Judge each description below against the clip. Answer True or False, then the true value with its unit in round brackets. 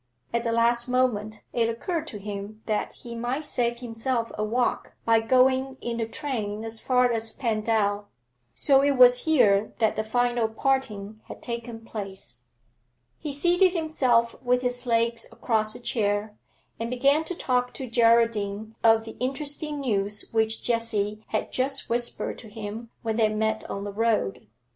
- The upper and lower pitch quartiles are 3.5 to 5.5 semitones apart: False (2.6 semitones)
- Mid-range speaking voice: False (230 Hz)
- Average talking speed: True (160 wpm)